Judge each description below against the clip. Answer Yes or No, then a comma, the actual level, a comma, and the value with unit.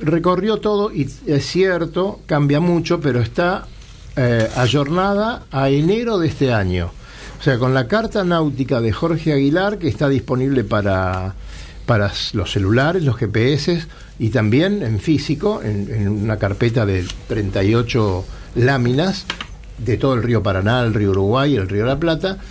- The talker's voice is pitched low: Yes, low, 130 Hz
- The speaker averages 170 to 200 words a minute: No, average, 155 wpm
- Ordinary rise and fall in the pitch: No, wide, 7.4 semitones